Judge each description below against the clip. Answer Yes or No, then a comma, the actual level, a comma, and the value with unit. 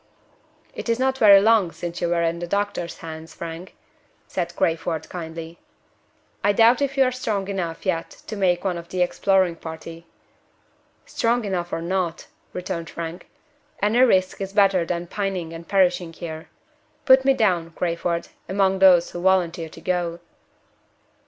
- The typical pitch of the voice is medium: Yes, medium, 180 Hz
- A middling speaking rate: Yes, average, 160 wpm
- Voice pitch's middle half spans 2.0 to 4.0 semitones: Yes, average, 3.0 semitones